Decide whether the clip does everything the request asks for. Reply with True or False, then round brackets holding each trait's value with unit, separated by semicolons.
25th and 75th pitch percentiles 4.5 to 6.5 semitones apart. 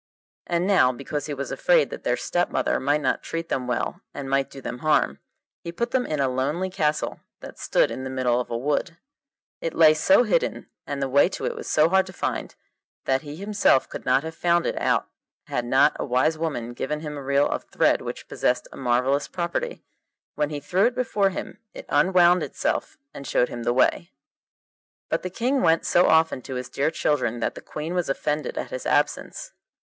True (5.0 semitones)